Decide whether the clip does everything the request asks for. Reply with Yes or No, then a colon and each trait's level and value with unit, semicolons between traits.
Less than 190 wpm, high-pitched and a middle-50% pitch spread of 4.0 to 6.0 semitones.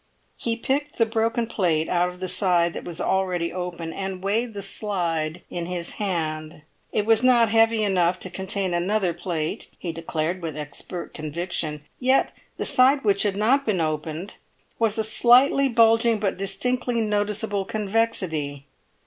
Yes: average, 155 wpm; high, 195 Hz; average, 4.7 semitones